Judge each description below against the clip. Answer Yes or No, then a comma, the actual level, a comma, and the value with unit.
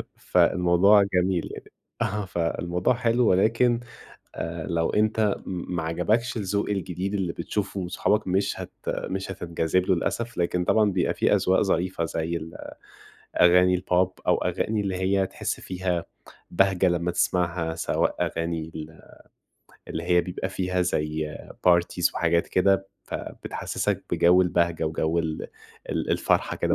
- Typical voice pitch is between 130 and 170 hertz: No, very low, 90 Hz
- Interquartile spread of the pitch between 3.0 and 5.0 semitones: No, narrow, 2.4 semitones